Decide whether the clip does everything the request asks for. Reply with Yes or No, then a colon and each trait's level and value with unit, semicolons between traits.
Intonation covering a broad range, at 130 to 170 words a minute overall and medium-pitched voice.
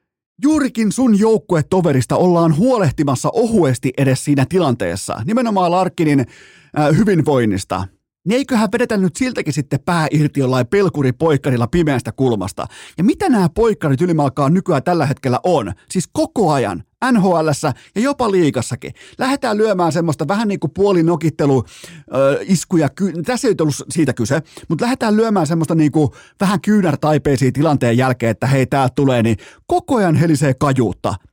Yes: wide, 6.4 semitones; average, 140 wpm; medium, 160 Hz